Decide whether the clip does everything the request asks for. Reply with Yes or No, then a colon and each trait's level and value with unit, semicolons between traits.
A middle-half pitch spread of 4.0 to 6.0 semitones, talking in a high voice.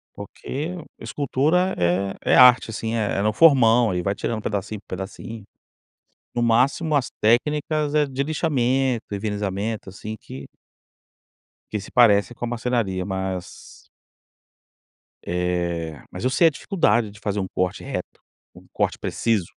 No: average, 5.0 semitones; low, 110 Hz